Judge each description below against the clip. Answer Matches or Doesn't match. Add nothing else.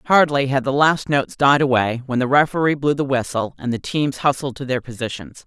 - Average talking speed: Doesn't match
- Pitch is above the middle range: Doesn't match